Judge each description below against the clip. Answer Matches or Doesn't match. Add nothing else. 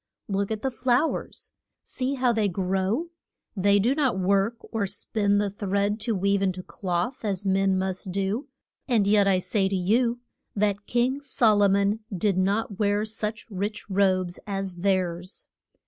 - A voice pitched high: Matches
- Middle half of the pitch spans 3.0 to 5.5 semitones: Doesn't match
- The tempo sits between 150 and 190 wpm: Matches